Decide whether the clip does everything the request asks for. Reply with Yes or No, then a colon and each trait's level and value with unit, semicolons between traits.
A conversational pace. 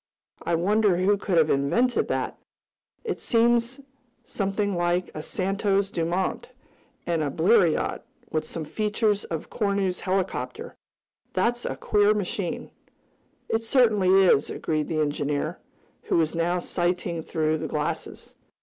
No: slow, 125 wpm